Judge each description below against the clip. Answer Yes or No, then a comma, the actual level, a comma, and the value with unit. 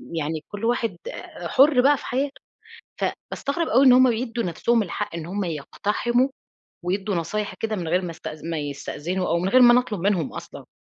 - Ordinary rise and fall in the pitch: No, wide, 6.3 semitones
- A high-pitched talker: Yes, high, 205 Hz